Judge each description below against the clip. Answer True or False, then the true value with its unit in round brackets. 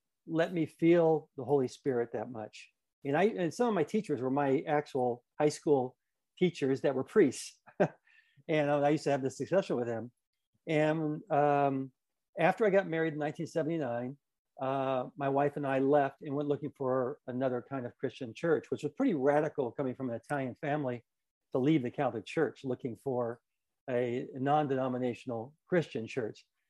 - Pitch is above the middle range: False (140 Hz)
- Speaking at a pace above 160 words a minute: True (170 wpm)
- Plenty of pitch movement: False (3.2 semitones)